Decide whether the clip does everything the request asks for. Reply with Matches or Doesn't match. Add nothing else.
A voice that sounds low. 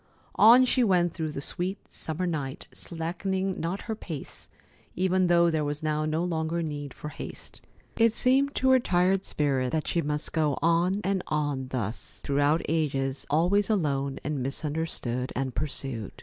Doesn't match